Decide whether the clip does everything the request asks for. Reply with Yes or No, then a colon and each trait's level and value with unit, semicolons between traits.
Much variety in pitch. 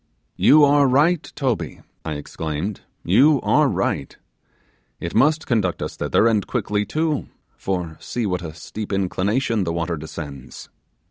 Yes: wide, 8.1 semitones